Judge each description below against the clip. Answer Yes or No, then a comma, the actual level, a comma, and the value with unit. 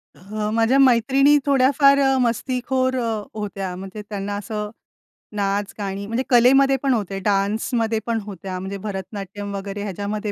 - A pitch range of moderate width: Yes, average, 4.2 semitones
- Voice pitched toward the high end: Yes, high, 210 Hz